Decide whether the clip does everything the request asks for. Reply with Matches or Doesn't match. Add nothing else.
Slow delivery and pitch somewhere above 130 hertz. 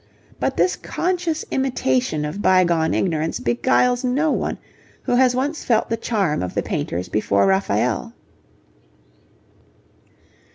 Matches